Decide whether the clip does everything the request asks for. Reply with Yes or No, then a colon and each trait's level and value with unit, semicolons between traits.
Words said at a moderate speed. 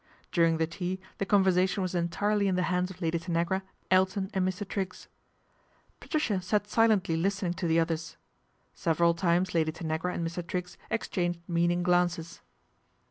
Yes: average, 160 wpm